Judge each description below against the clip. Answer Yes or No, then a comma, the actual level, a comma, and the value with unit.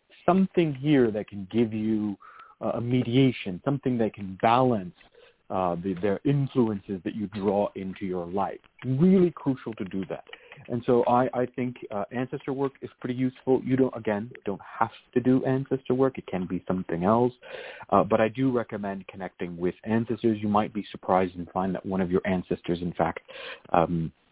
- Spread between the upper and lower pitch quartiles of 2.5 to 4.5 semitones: No, average, 5.0 semitones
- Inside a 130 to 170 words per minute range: No, average, 185 wpm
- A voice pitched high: No, low, 110 Hz